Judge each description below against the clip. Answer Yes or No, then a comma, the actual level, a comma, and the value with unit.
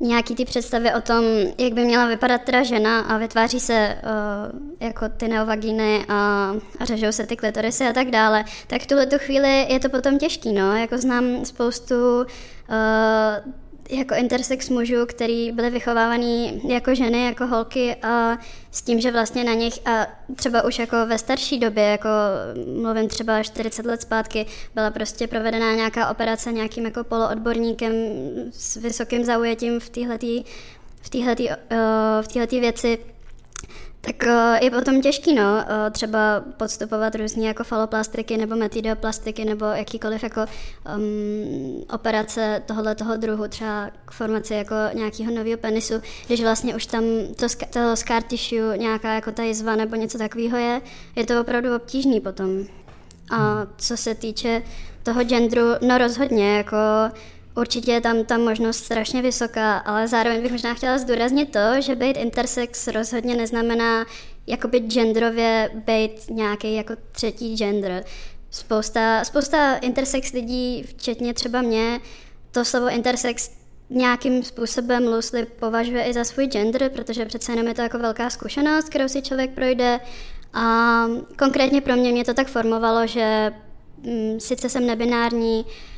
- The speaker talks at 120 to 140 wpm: No, average, 150 wpm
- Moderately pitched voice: No, high, 230 Hz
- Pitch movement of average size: No, narrow, 1.8 semitones